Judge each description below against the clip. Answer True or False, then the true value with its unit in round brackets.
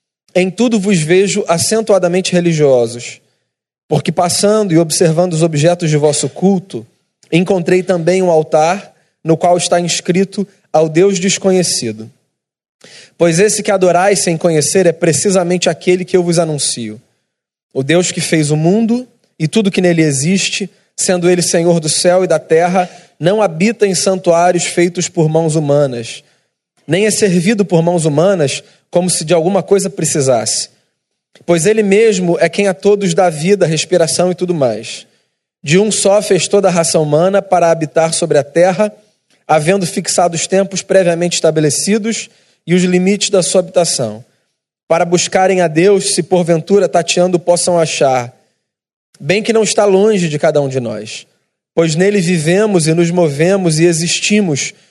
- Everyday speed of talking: True (155 wpm)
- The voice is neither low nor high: True (175 Hz)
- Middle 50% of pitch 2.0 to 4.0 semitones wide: True (3.0 semitones)